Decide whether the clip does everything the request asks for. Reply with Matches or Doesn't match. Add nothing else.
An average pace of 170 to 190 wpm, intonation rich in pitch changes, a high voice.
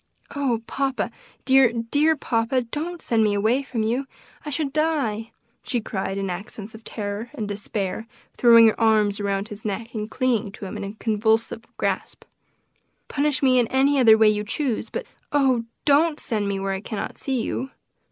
Doesn't match